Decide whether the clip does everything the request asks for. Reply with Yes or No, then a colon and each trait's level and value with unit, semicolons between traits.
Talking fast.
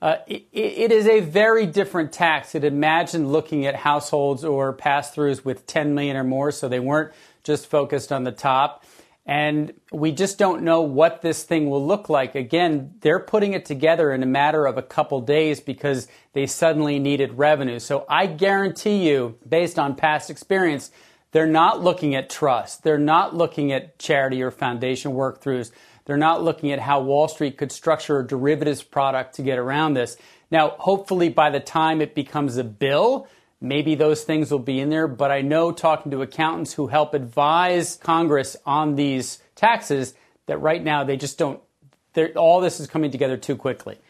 No: average, 185 wpm